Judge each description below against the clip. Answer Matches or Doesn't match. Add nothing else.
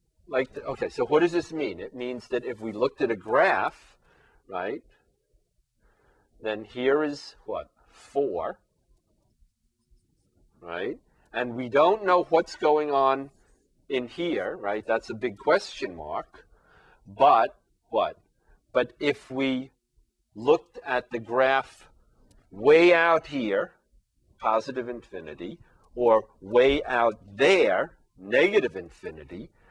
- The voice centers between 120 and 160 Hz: Matches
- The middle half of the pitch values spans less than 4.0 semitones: Doesn't match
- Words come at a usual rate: Doesn't match